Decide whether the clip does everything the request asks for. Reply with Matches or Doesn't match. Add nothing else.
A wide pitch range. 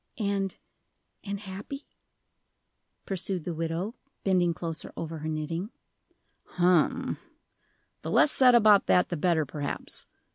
Doesn't match